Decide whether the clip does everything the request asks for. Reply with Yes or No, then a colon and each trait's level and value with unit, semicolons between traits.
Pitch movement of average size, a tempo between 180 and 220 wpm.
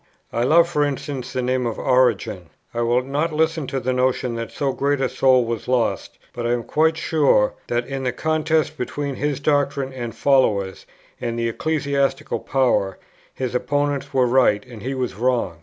Yes: average, 3.1 semitones; average, 185 wpm